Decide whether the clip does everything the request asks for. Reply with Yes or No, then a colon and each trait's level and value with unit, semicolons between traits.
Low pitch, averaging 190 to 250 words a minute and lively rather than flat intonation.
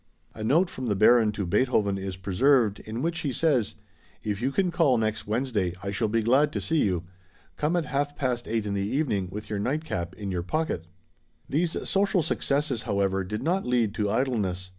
Yes: low, 115 Hz; average, 200 wpm; wide, 6.2 semitones